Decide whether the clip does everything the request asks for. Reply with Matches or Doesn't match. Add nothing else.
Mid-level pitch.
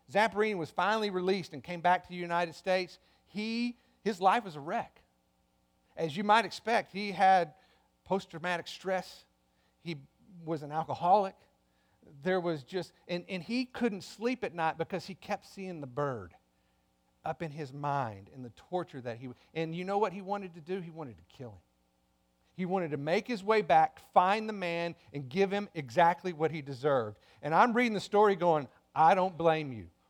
Matches